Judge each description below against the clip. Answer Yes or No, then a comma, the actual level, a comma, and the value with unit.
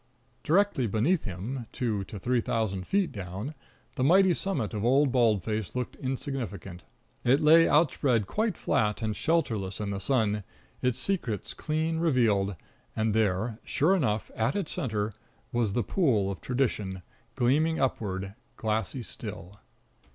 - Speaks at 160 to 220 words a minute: No, average, 145 wpm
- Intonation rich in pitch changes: Yes, wide, 5.7 semitones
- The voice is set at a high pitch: No, low, 115 Hz